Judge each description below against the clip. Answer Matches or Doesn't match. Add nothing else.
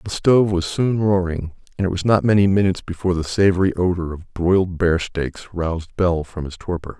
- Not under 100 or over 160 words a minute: Doesn't match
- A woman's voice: Doesn't match